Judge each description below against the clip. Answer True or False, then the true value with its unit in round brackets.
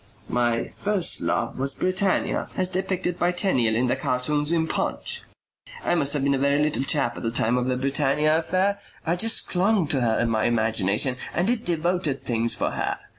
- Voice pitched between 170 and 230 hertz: False (145 Hz)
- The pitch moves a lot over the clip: True (6.3 semitones)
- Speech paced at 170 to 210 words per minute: True (195 wpm)